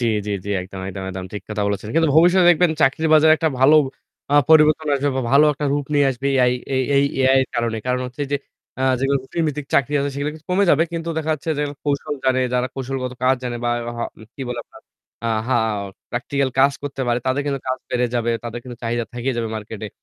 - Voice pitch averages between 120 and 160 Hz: Yes, low, 135 Hz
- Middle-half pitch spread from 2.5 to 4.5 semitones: Yes, average, 3.5 semitones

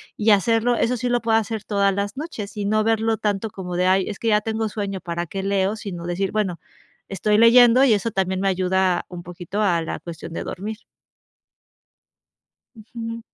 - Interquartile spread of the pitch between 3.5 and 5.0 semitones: No, average, 2.9 semitones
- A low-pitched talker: No, high, 205 Hz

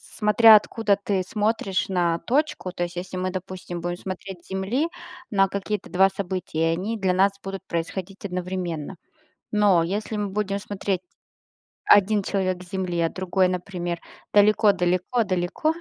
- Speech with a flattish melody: Yes, narrow, 2.3 semitones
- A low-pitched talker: No, high, 190 Hz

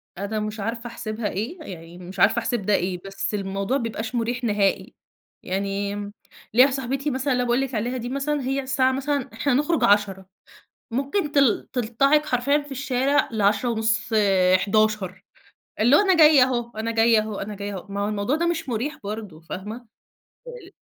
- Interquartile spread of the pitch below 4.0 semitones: No, average, 4.7 semitones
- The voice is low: No, high, 230 Hz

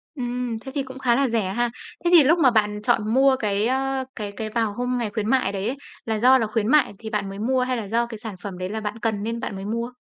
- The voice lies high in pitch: Yes, high, 230 Hz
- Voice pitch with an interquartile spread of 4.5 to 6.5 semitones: No, average, 3.3 semitones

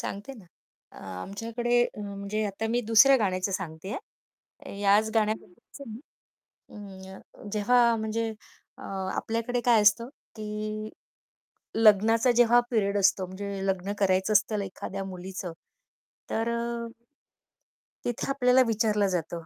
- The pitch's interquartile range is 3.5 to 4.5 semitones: No, average, 2.7 semitones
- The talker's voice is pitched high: Yes, high, 215 Hz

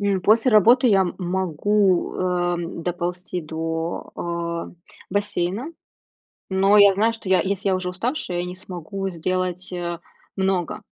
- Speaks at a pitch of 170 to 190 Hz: Yes, medium, 185 Hz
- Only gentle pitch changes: Yes, narrow, 2.3 semitones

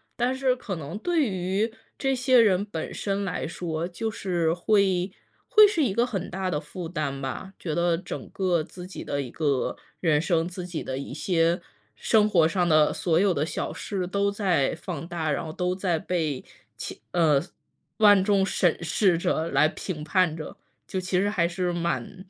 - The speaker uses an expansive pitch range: No, average, 3.5 semitones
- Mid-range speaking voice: Yes, medium, 180 Hz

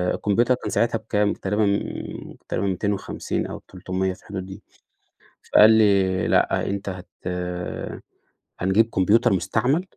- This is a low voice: Yes, low, 100 Hz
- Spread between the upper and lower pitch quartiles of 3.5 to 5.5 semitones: No, average, 2.7 semitones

